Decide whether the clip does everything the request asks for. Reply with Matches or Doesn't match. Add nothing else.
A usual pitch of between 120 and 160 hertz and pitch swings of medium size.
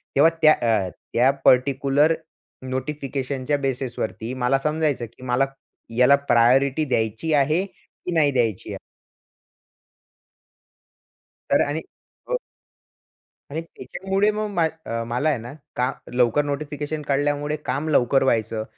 Matches